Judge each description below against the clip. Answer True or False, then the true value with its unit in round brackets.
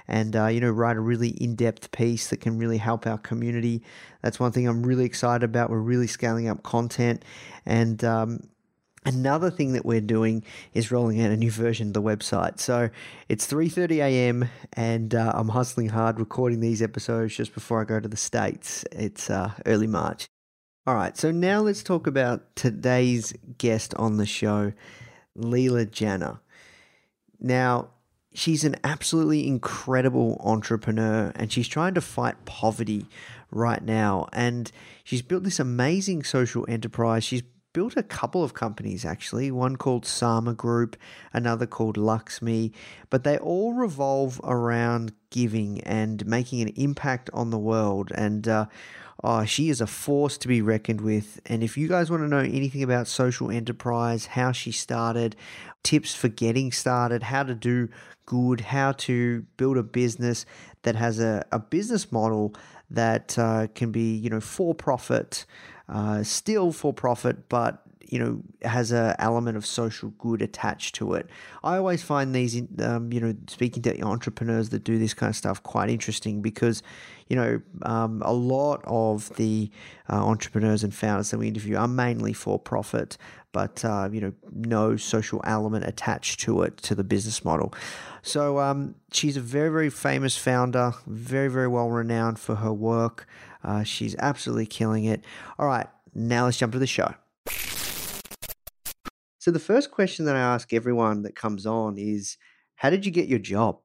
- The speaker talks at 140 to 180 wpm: True (170 wpm)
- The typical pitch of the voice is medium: False (115 Hz)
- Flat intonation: True (2.3 semitones)